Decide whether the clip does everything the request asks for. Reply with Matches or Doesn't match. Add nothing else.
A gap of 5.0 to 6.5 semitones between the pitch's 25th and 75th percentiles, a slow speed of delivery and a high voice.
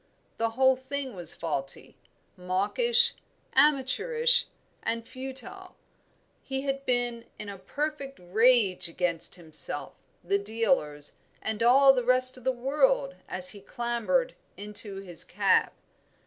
Matches